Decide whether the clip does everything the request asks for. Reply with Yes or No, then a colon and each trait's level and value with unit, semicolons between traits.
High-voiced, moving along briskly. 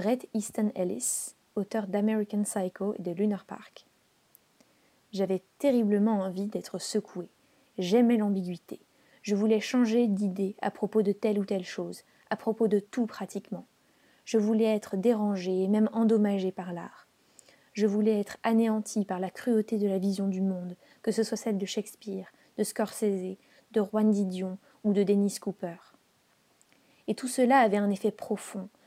No: high, 210 Hz; average, 160 wpm